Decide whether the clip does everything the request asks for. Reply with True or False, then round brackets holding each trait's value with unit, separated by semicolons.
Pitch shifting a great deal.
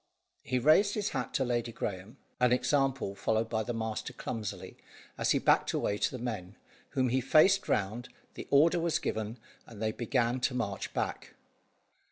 False (3.5 semitones)